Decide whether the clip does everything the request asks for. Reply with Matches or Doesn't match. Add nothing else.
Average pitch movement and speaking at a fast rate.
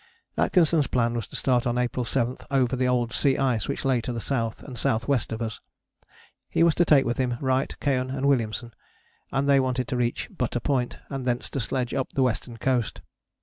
Doesn't match